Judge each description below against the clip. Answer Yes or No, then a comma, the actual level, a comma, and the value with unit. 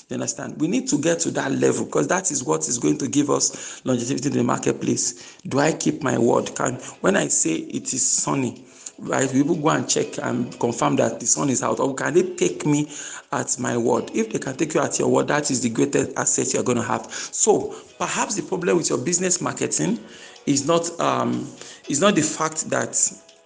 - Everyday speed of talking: No, fast, 230 wpm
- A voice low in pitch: No, medium, 150 Hz